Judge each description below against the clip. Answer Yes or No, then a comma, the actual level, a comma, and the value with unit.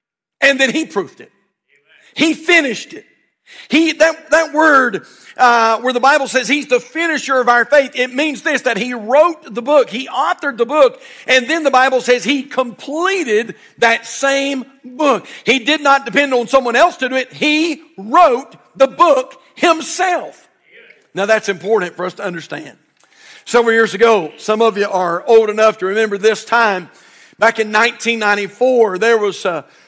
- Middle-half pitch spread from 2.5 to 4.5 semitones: No, average, 5.1 semitones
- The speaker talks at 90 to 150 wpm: No, average, 175 wpm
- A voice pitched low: No, very high, 255 Hz